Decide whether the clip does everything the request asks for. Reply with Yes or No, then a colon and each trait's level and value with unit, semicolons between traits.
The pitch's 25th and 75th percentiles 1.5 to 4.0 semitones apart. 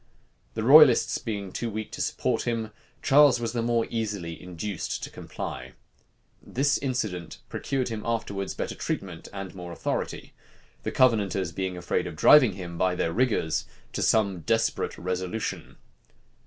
No: average, 4.5 semitones